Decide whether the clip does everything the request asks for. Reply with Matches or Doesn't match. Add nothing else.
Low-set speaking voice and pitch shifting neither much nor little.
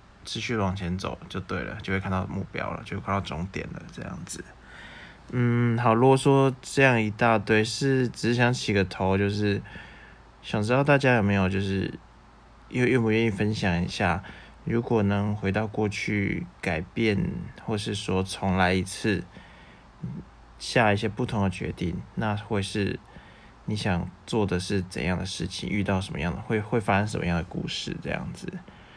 Matches